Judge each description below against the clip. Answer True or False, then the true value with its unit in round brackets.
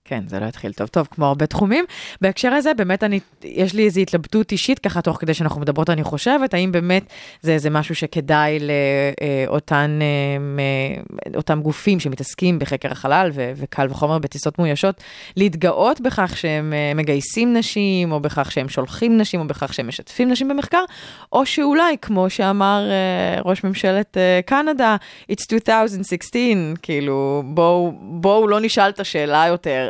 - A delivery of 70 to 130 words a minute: False (150 wpm)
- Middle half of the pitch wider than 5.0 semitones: True (5.5 semitones)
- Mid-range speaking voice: True (175 Hz)